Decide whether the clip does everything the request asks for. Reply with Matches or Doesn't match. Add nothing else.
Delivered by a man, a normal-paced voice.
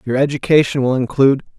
Matches